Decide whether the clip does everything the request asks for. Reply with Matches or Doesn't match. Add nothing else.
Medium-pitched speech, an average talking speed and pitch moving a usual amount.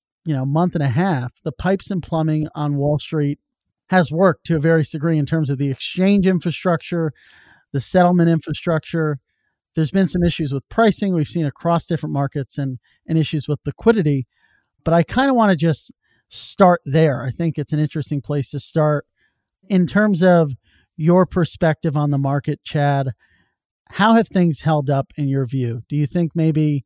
Matches